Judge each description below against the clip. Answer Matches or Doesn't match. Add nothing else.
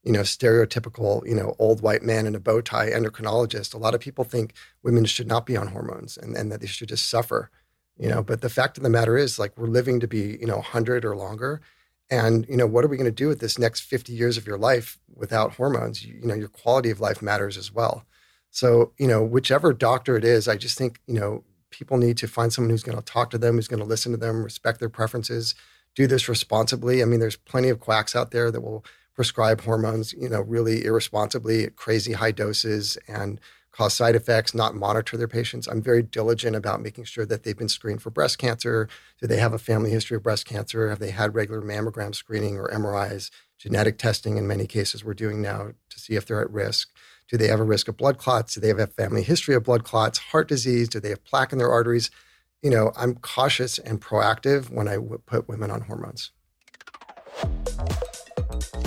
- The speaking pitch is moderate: Doesn't match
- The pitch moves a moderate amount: Doesn't match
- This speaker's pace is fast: Matches